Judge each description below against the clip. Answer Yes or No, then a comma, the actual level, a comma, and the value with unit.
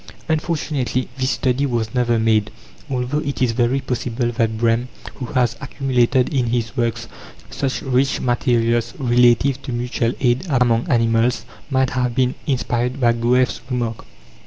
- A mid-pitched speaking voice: No, low, 125 Hz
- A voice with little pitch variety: Yes, narrow, 1.9 semitones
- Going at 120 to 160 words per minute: Yes, average, 145 wpm